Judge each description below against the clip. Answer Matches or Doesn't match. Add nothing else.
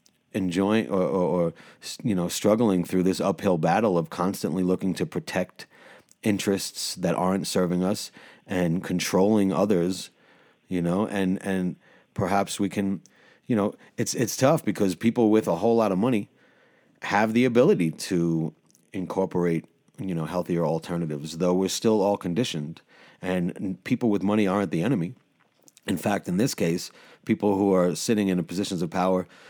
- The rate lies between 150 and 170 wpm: Matches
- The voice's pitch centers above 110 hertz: Doesn't match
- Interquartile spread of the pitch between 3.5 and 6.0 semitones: Doesn't match